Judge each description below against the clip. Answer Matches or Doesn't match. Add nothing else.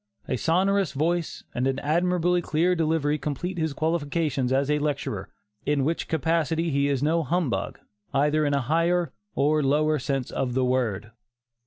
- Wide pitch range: Doesn't match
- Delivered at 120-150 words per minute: Doesn't match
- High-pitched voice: Doesn't match